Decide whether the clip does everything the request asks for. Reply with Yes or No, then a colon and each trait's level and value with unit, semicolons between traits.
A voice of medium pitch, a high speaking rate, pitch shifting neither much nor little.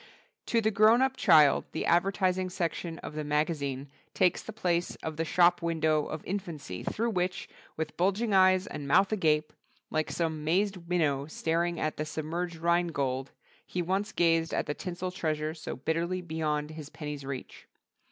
No: medium, 165 Hz; average, 170 wpm; average, 3.1 semitones